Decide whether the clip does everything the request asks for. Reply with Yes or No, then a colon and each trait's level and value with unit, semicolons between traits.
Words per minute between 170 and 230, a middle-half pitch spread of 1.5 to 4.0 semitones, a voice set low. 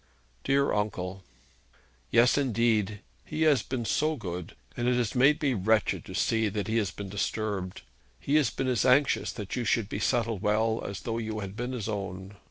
Yes: average, 190 wpm; average, 3.6 semitones; low, 110 Hz